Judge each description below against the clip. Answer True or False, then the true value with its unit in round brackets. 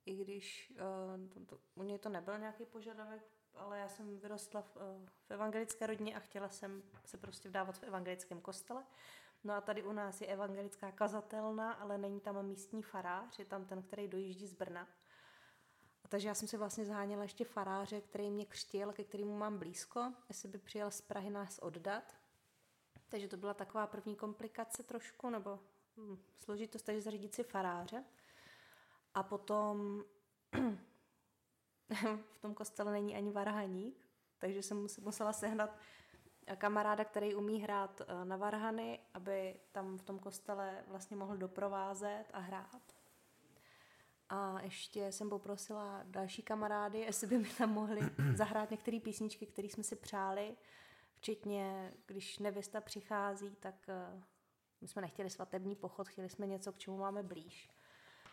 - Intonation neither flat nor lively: False (1.6 semitones)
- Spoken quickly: False (155 wpm)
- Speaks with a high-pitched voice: True (205 Hz)